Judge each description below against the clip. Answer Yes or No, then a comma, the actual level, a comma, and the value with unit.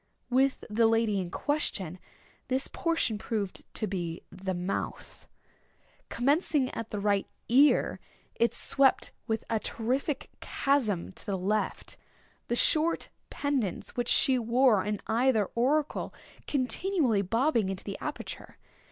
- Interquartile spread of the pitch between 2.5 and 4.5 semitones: No, average, 5.0 semitones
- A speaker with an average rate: No, slow, 125 wpm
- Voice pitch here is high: Yes, high, 230 Hz